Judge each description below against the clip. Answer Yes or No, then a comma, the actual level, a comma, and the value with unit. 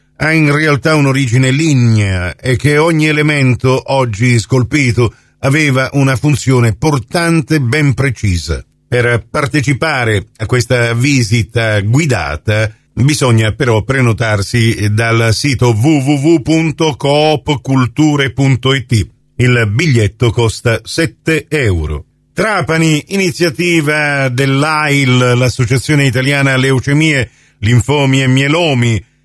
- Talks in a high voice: No, low, 135 Hz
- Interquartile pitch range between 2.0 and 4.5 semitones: Yes, average, 4.1 semitones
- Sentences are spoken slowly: Yes, slow, 90 wpm